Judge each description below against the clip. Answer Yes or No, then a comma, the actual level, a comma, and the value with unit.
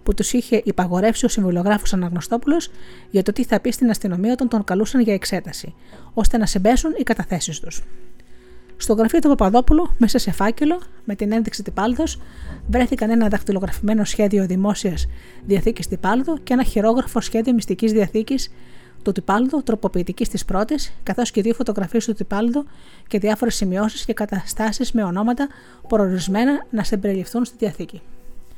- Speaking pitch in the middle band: No, high, 215 Hz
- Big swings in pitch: No, average, 3.7 semitones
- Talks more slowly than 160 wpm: Yes, average, 150 wpm